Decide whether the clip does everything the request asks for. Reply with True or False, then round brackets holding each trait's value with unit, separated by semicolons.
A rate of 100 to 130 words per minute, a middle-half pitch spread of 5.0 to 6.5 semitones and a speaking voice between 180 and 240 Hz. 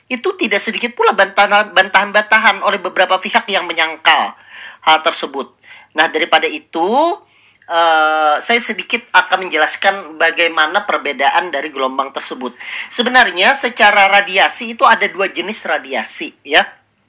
True (125 wpm; 5.5 semitones; 190 Hz)